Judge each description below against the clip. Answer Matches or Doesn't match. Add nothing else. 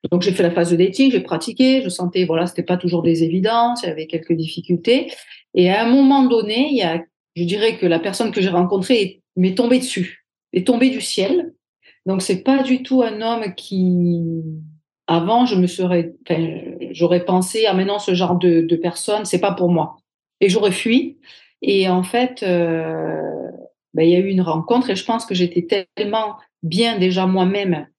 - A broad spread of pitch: Doesn't match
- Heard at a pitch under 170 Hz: Doesn't match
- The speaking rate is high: Doesn't match